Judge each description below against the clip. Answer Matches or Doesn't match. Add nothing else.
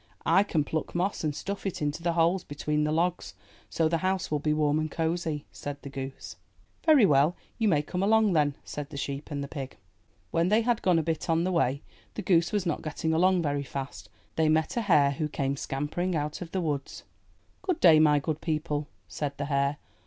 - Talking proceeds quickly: Matches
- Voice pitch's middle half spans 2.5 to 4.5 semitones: Matches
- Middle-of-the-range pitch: Matches